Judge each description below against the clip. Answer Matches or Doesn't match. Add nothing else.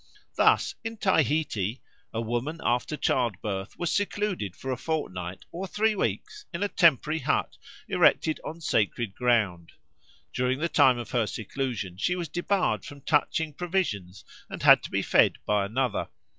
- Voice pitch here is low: Matches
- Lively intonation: Matches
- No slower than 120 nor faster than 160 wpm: Matches